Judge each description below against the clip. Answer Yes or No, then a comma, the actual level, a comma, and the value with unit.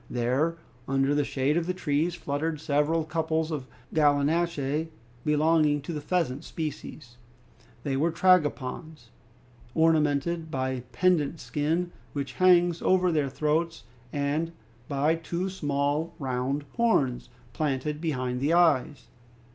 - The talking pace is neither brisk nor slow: No, slow, 125 wpm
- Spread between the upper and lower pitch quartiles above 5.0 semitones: No, average, 2.9 semitones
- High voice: No, medium, 150 Hz